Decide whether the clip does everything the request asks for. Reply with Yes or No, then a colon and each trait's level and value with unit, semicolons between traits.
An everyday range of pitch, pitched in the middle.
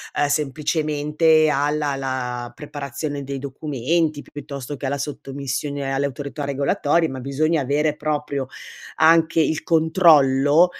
No: narrow, 2.1 semitones; medium, 145 Hz